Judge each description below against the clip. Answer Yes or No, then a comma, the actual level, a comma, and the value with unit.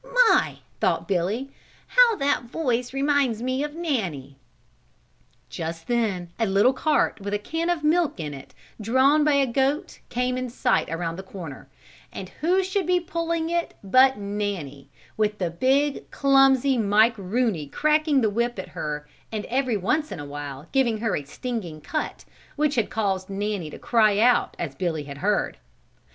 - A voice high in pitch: Yes, high, 235 Hz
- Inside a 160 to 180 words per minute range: Yes, average, 170 wpm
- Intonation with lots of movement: Yes, wide, 7.0 semitones